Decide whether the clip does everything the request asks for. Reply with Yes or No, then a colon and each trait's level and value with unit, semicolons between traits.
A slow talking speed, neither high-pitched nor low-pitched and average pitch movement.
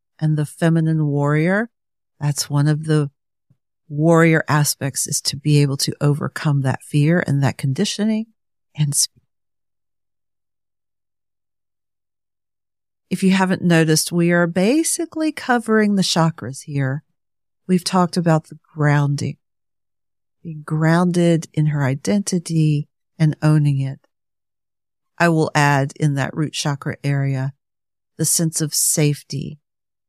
Yes: slow, 120 wpm; medium, 150 Hz; average, 3.7 semitones